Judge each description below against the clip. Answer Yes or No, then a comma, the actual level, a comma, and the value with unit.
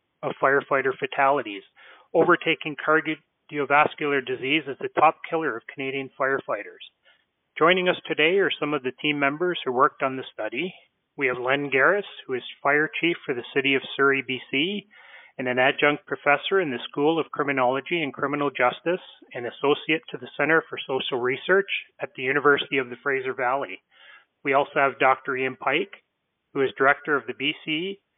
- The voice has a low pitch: No, medium, 145 Hz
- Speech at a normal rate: Yes, average, 170 wpm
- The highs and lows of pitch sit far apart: No, average, 3.3 semitones